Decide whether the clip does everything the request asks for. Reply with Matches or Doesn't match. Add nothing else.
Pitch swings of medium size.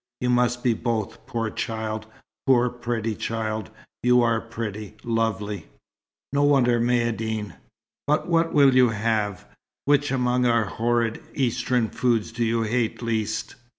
Doesn't match